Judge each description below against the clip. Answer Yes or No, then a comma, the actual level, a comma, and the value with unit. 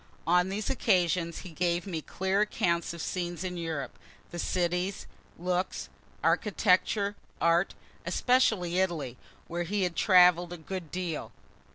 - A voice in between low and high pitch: Yes, medium, 180 Hz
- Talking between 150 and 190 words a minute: No, slow, 135 wpm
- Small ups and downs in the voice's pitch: Yes, narrow, 1.9 semitones